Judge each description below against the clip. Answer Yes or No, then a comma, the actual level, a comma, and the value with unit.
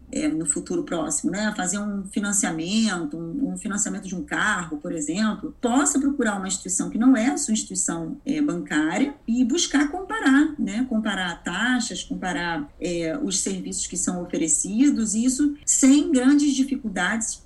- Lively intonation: Yes, wide, 6.8 semitones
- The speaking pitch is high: Yes, high, 230 Hz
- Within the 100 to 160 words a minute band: Yes, average, 155 wpm